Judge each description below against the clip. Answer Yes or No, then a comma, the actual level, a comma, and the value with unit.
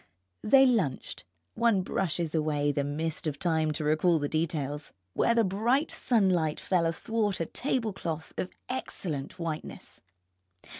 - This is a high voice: No, medium, 165 Hz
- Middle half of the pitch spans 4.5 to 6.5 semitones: Yes, wide, 5.4 semitones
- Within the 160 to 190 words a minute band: No, slow, 135 wpm